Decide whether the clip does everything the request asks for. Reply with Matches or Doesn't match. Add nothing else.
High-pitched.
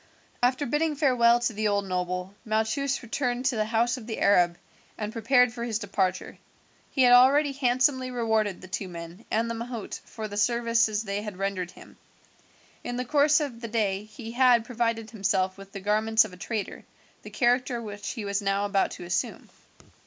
Matches